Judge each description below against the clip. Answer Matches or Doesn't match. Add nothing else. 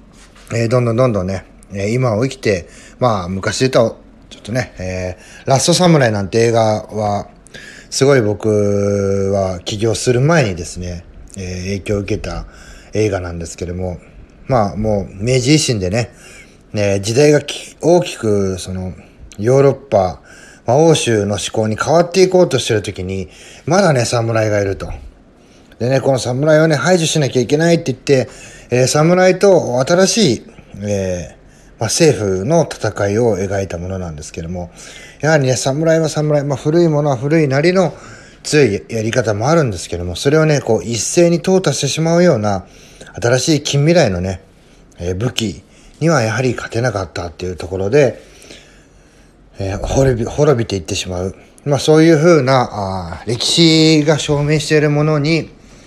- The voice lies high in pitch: Doesn't match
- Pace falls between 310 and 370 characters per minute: Matches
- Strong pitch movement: Matches